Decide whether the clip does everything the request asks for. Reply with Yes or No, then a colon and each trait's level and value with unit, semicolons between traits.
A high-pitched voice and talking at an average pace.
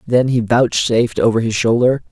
No: low, 120 Hz; average, 170 wpm